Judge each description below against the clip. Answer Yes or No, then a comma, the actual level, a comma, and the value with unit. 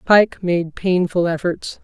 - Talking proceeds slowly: Yes, slow, 130 wpm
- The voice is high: No, medium, 175 Hz